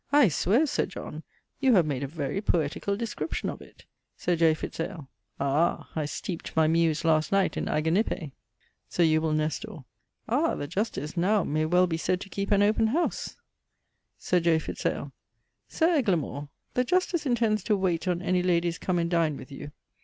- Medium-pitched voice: Yes, medium, 175 Hz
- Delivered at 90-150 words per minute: No, average, 185 wpm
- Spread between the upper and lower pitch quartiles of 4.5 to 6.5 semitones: Yes, average, 4.8 semitones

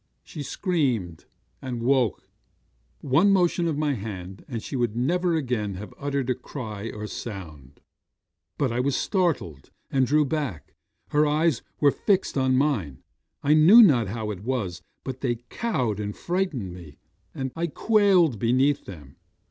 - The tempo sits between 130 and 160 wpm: Yes, average, 150 wpm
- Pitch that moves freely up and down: Yes, wide, 6.3 semitones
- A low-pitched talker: Yes, low, 130 Hz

